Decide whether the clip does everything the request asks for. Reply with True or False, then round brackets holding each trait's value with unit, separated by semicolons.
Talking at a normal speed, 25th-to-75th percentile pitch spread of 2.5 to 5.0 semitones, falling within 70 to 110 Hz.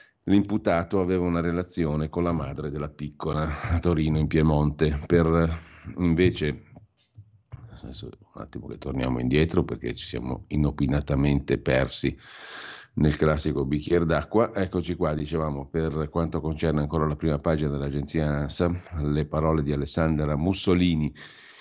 True (130 wpm; 2.8 semitones; 80 Hz)